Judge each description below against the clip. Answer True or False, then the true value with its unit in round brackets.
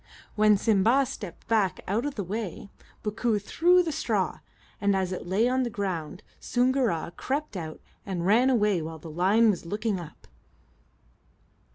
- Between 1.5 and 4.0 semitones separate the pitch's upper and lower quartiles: False (4.6 semitones)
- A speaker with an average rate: True (165 wpm)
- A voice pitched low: False (210 Hz)